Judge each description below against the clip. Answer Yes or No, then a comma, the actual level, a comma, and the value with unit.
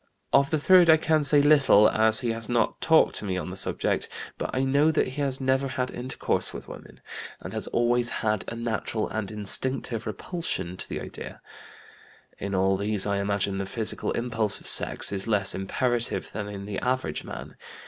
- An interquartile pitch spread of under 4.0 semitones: No, average, 4.6 semitones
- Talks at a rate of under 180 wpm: No, average, 195 wpm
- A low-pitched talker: Yes, low, 115 Hz